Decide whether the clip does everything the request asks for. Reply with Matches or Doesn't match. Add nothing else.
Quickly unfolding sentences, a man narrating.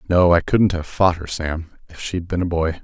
Matches